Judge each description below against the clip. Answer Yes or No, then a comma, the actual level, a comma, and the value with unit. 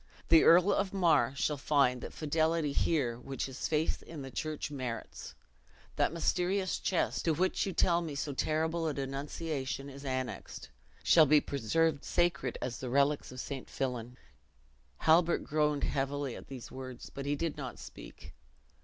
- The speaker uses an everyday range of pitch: Yes, average, 3.5 semitones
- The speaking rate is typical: Yes, average, 160 wpm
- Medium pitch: Yes, medium, 145 Hz